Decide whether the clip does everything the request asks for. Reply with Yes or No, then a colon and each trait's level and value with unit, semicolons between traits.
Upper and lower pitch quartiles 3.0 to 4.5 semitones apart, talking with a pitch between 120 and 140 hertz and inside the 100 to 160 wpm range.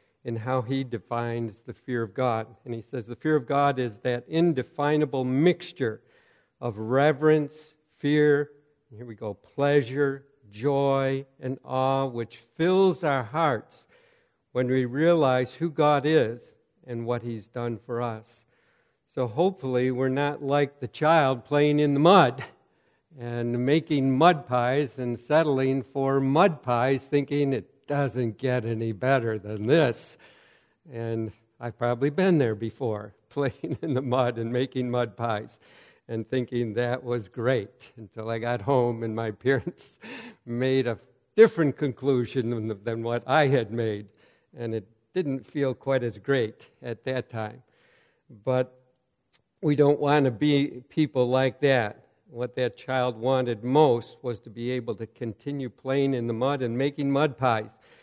Yes: average, 3.3 semitones; low, 130 Hz; average, 155 wpm